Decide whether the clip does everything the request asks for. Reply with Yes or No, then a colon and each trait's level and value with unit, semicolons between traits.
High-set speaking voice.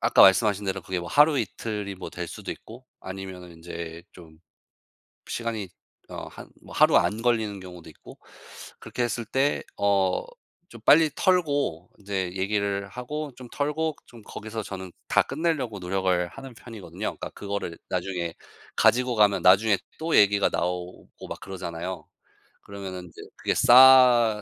No: low, 100 Hz